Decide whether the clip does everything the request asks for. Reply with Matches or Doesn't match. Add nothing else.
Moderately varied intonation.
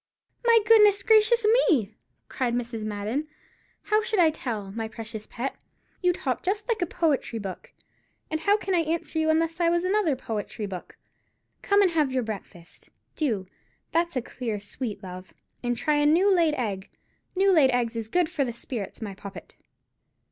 Doesn't match